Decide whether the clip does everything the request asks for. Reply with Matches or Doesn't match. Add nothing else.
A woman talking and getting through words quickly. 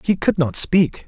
Doesn't match